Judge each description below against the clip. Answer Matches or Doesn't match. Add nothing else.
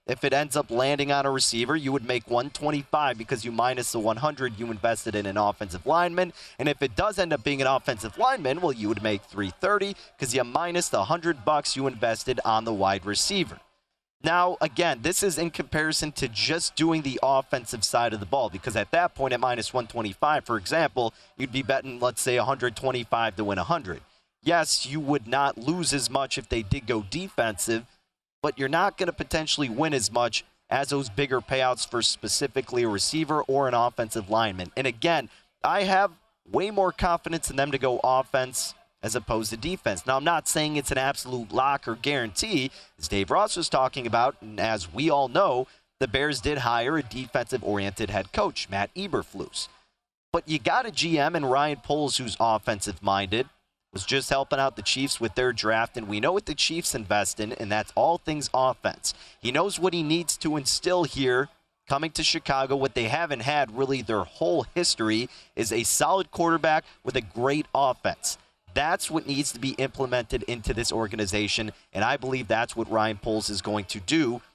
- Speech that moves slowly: Doesn't match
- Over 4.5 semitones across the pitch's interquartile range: Matches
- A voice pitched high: Doesn't match